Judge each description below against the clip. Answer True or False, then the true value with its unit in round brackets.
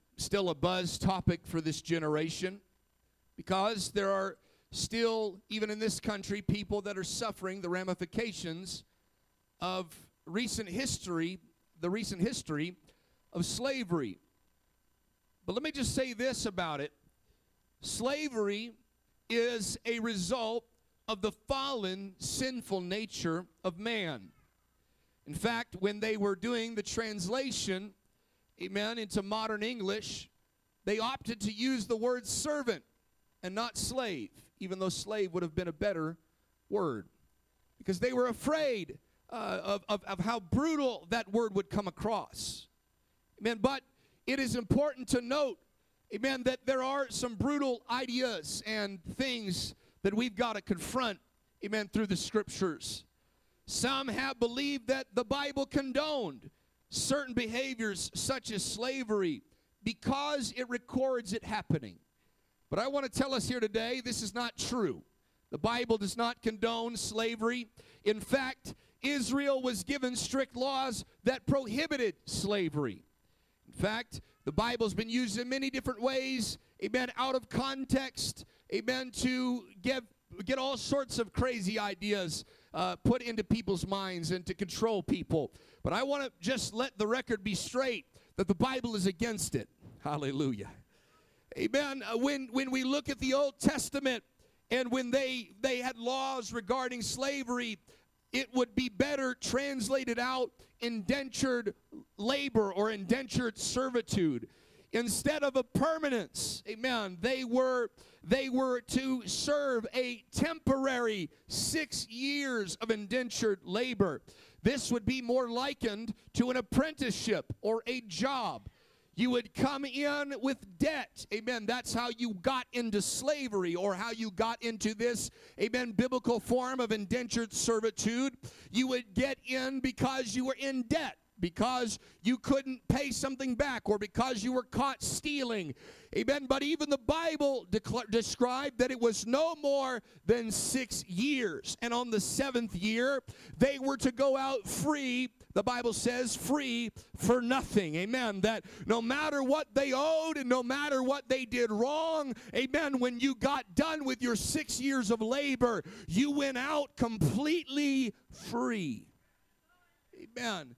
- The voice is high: True (240 Hz)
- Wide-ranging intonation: False (4.0 semitones)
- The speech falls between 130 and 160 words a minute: True (140 wpm)